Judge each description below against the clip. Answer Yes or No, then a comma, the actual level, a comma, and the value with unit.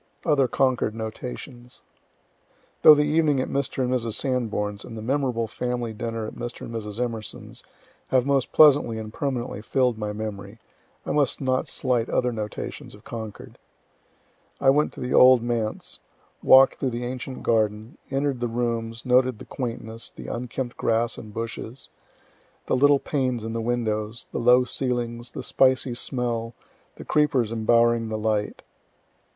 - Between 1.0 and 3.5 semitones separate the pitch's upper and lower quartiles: Yes, narrow, 2.4 semitones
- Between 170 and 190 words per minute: No, average, 155 wpm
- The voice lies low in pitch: Yes, low, 120 Hz